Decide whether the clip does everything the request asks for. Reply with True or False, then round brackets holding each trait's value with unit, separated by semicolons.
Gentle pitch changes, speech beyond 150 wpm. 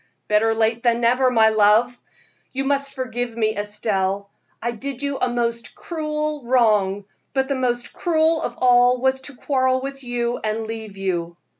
False (3.3 semitones; 165 wpm)